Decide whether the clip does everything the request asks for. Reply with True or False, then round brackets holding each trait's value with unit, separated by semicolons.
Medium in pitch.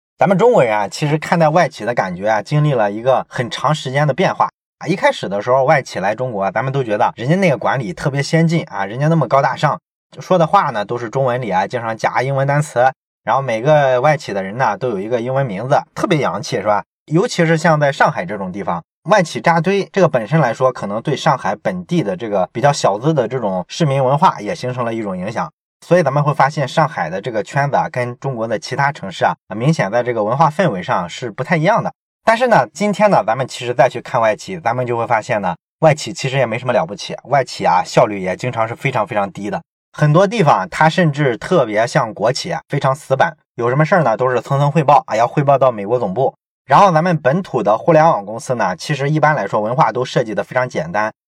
True (145 Hz)